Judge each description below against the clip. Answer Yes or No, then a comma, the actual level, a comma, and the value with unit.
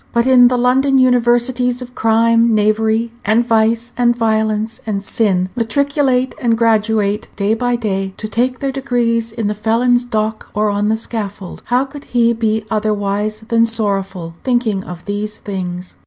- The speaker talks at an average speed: Yes, average, 160 wpm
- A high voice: Yes, high, 225 Hz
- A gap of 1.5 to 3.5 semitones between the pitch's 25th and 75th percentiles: Yes, narrow, 2.5 semitones